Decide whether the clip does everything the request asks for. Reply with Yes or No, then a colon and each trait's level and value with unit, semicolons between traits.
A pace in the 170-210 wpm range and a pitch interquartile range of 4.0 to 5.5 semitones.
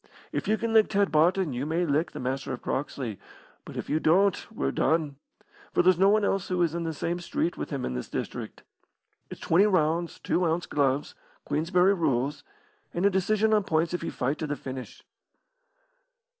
Yes: average, 200 wpm; average, 4.4 semitones